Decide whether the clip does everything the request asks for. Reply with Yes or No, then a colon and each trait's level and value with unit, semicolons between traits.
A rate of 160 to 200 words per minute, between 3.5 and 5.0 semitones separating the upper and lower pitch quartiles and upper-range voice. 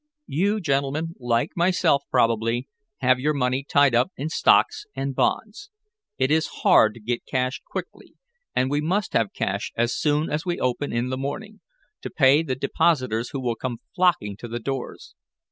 No: average, 175 wpm; average, 4.4 semitones; low, 135 Hz